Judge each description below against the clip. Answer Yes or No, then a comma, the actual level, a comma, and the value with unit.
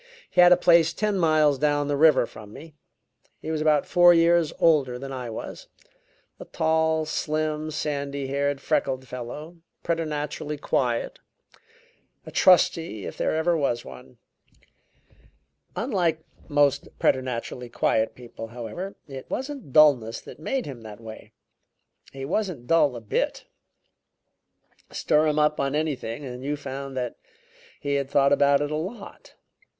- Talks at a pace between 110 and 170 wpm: Yes, average, 145 wpm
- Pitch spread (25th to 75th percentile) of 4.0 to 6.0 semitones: No, average, 3.5 semitones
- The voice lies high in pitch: No, medium, 145 Hz